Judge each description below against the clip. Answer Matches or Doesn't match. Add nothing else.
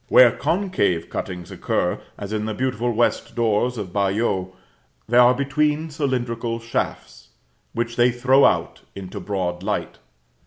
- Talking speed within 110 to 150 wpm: Matches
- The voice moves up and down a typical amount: Matches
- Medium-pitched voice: Doesn't match